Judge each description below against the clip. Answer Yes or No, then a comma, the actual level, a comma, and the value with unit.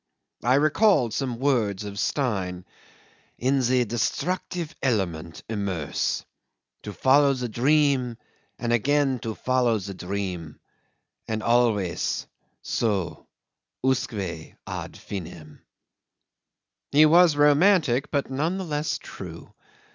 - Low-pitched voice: Yes, low, 120 Hz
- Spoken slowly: Yes, slow, 110 wpm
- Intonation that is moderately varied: No, wide, 6.0 semitones